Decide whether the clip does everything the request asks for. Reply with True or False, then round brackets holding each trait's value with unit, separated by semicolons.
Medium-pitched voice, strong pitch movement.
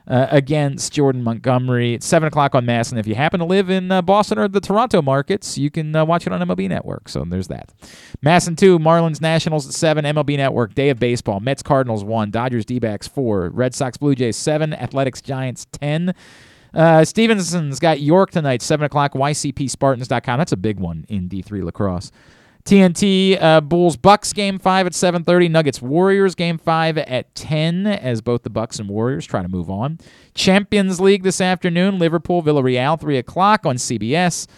True (145 Hz; 6.2 semitones)